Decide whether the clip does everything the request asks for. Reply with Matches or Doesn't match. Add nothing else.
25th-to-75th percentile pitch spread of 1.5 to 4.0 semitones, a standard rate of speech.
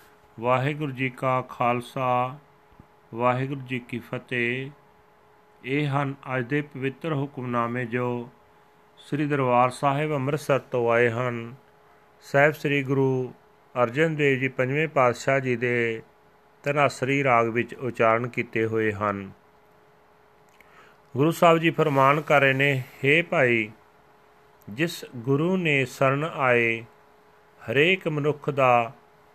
Matches